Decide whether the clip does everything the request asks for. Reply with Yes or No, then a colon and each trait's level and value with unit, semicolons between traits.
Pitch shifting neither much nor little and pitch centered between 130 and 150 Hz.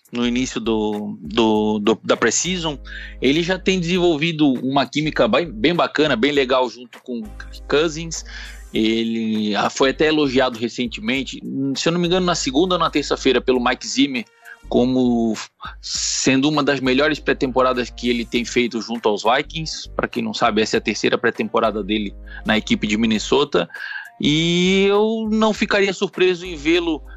No: wide, 7.1 semitones; low, 135 Hz